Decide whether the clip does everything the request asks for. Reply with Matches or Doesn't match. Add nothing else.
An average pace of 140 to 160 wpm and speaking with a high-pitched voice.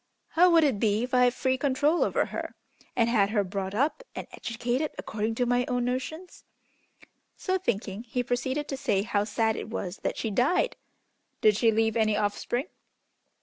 Doesn't match